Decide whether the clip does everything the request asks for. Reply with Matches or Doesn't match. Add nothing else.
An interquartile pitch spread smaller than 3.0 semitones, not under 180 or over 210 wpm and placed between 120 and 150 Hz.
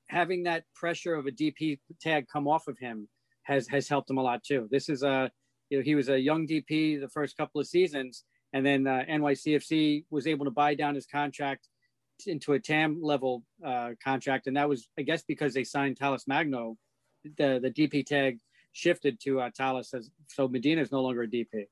Matches